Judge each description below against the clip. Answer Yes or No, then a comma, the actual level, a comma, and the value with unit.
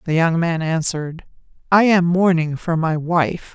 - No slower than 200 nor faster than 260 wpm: No, average, 170 wpm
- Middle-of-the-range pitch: Yes, medium, 165 Hz